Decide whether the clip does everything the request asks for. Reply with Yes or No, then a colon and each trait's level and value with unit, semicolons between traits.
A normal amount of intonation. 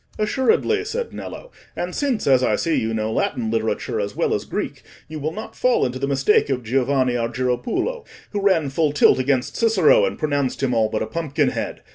No: wide, 8.4 semitones